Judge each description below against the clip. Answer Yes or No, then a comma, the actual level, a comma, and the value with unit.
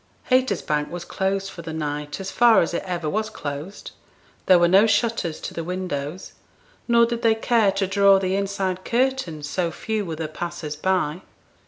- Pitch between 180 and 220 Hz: Yes, medium, 185 Hz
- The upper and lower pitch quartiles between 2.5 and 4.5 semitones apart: Yes, average, 4.1 semitones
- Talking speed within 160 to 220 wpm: Yes, average, 180 wpm